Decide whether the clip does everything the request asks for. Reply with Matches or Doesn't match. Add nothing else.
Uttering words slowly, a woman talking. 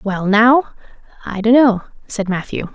Matches